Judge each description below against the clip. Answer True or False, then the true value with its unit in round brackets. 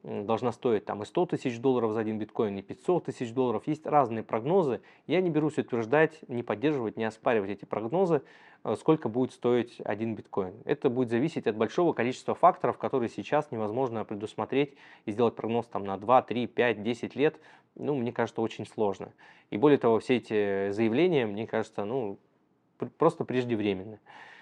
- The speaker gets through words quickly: True (170 wpm)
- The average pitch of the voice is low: True (120 Hz)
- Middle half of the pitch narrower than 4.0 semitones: True (3.6 semitones)